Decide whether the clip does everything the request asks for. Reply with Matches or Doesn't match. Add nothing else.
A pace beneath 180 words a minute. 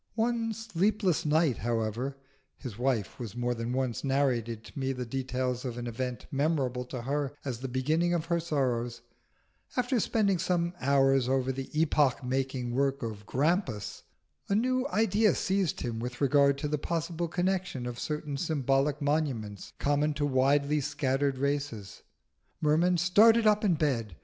Matches